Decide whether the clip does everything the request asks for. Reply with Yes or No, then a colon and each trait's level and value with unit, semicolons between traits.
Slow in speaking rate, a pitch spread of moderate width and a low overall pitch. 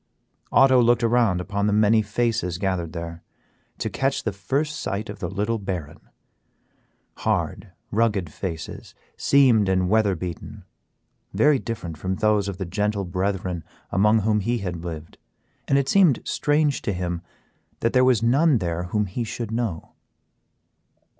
No: average, 150 wpm; average, 4.4 semitones; low, 105 Hz